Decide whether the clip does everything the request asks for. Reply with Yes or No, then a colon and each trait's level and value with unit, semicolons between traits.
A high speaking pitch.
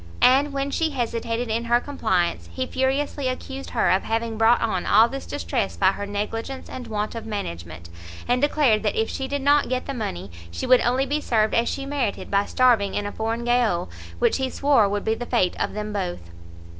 Yes: high, 230 Hz